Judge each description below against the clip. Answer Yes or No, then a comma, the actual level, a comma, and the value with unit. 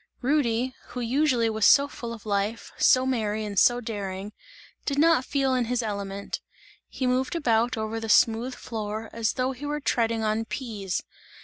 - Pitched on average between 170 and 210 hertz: No, high, 230 Hz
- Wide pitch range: No, average, 3.0 semitones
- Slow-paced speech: No, average, 175 wpm